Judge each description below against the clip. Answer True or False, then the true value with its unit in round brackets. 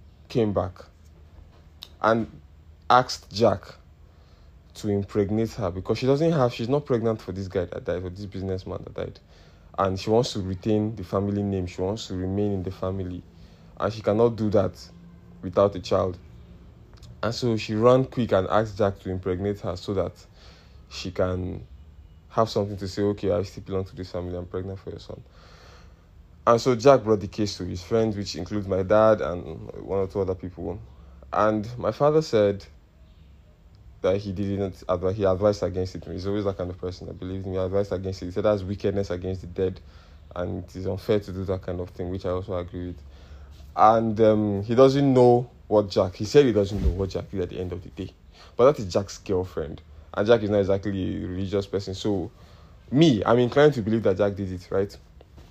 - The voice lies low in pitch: True (95 Hz)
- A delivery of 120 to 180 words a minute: False (205 wpm)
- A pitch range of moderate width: True (3.1 semitones)